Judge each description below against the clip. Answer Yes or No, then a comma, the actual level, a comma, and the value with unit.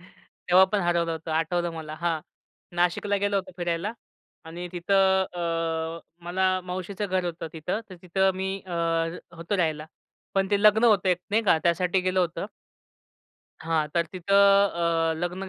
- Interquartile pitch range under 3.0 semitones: Yes, narrow, 2.4 semitones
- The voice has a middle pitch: Yes, medium, 180 Hz